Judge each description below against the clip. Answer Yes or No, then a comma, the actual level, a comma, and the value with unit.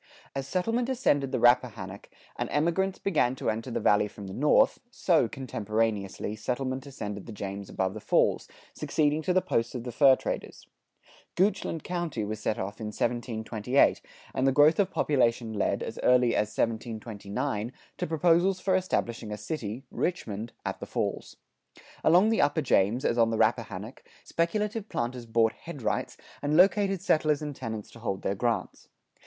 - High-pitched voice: No, low, 125 Hz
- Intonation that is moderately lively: No, wide, 6.4 semitones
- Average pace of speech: Yes, average, 165 wpm